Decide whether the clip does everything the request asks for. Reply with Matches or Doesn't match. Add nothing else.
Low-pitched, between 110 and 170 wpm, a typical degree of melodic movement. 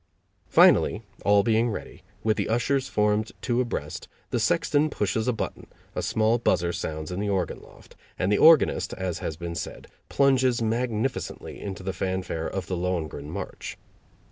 Matches